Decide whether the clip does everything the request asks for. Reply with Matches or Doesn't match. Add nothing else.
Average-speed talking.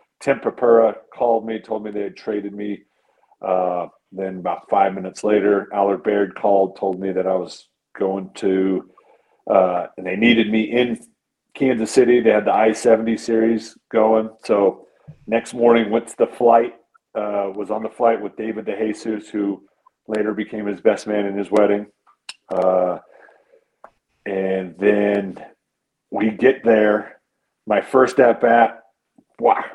Matches